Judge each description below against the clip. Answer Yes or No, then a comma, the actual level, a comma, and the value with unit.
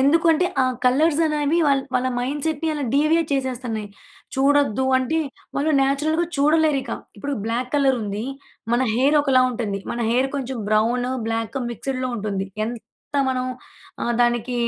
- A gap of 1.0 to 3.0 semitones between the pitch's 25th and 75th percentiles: No, average, 3.4 semitones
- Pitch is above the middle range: Yes, very high, 265 Hz